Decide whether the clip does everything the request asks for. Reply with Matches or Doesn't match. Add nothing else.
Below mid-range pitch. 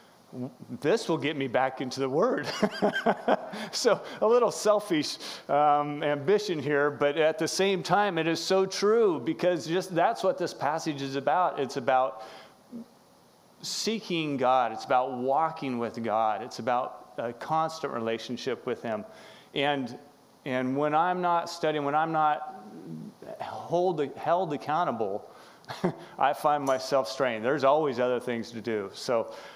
Doesn't match